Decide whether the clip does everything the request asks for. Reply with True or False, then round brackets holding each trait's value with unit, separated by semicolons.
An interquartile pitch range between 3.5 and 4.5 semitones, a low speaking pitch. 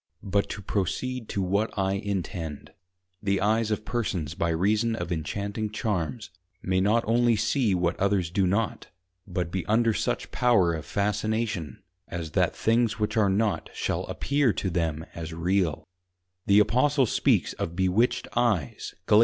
True (3.8 semitones; 100 Hz)